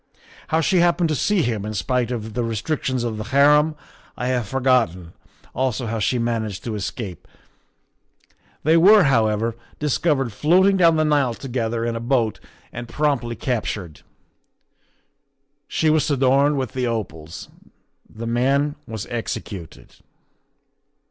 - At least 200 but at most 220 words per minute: No, slow, 135 wpm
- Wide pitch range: No, average, 4.7 semitones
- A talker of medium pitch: No, low, 125 Hz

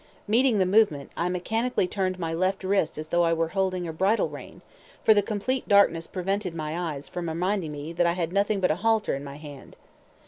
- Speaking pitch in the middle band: Yes, medium, 180 Hz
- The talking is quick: Yes, fast, 215 wpm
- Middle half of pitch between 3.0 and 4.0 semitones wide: Yes, average, 3.6 semitones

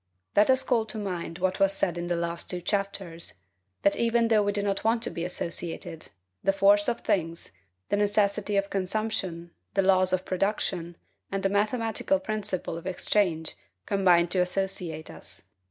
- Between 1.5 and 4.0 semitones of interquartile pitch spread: Yes, average, 2.8 semitones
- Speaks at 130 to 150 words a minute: No, average, 170 wpm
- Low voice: No, high, 195 Hz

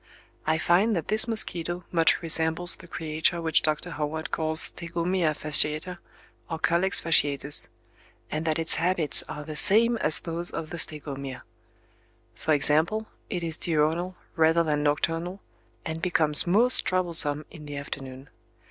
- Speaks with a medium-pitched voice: Yes, medium, 160 Hz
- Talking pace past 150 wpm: No, average, 145 wpm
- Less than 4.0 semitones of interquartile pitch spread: Yes, narrow, 2.4 semitones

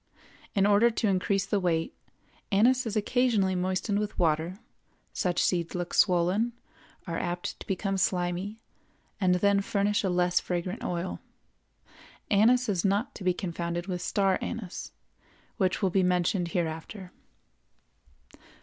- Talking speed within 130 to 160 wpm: Yes, slow, 135 wpm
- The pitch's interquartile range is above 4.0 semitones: No, narrow, 2.5 semitones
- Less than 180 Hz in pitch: No, medium, 185 Hz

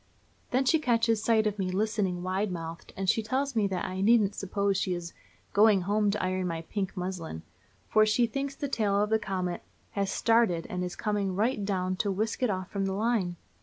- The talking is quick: Yes, fast, 210 wpm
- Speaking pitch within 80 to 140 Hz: No, high, 200 Hz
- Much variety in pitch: No, average, 3.0 semitones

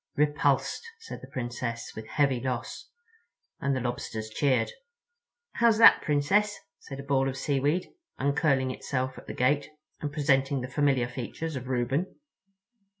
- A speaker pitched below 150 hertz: Yes, low, 135 Hz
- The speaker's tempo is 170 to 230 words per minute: No, average, 140 wpm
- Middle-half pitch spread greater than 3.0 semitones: No, average, 2.7 semitones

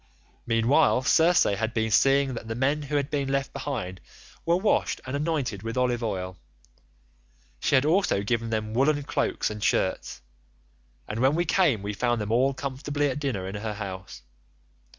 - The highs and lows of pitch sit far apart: No, average, 4.7 semitones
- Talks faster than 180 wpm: No, average, 170 wpm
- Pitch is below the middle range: Yes, low, 125 Hz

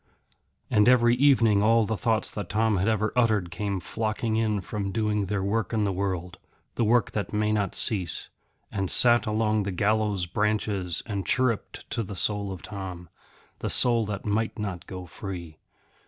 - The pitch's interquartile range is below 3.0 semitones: Yes, narrow, 2.4 semitones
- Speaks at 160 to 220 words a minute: Yes, average, 175 wpm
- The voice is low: Yes, low, 105 Hz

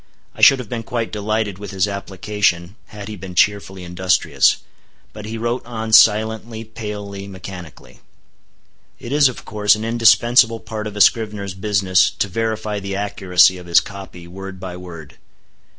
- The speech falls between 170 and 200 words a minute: No, average, 160 wpm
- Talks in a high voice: No, low, 105 Hz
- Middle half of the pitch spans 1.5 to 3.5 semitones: Yes, average, 2.8 semitones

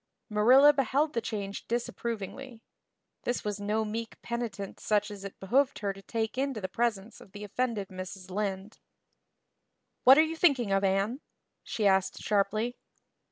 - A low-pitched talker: No, high, 215 Hz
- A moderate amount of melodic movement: Yes, average, 3.6 semitones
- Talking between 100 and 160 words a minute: Yes, average, 155 wpm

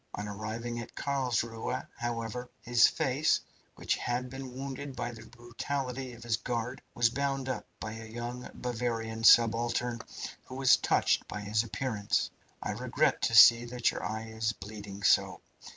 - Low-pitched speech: Yes, low, 120 Hz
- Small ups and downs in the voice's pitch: Yes, narrow, 2.1 semitones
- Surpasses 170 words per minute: No, average, 155 wpm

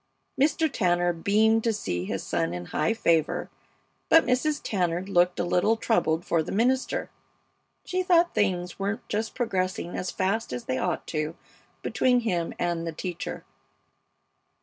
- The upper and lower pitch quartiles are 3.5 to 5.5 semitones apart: Yes, average, 5.0 semitones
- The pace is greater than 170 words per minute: No, average, 150 wpm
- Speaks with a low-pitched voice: No, medium, 185 Hz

